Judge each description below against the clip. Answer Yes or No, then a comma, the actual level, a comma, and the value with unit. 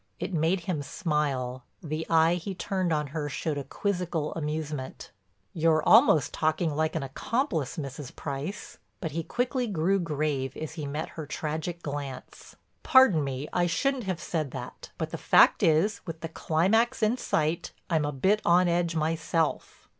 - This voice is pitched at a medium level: Yes, medium, 160 Hz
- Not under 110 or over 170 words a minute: Yes, average, 165 wpm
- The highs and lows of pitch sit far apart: No, average, 3.1 semitones